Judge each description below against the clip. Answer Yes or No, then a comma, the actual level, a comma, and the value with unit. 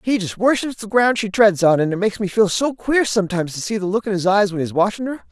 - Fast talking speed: Yes, fast, 305 wpm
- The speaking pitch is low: No, high, 205 Hz